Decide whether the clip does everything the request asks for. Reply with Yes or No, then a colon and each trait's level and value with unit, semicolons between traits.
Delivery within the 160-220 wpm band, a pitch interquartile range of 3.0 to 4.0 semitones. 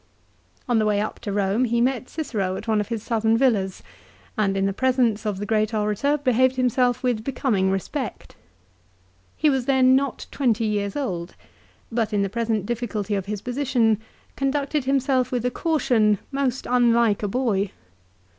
Yes: average, 170 wpm; average, 3.7 semitones